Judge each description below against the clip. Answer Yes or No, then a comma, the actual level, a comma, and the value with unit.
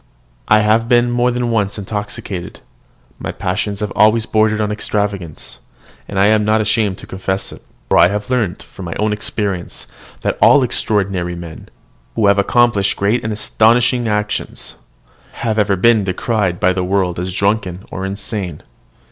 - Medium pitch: No, low, 105 Hz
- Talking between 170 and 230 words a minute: No, average, 160 wpm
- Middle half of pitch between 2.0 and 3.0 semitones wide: Yes, narrow, 2.4 semitones